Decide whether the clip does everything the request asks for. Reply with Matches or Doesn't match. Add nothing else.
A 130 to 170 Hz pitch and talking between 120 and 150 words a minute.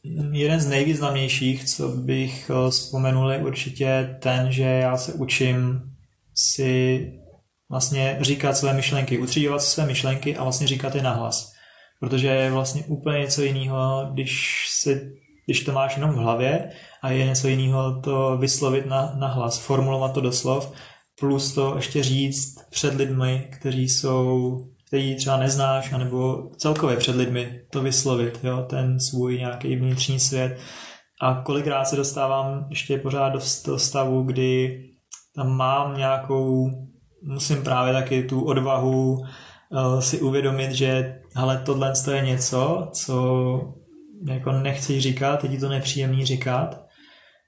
Matches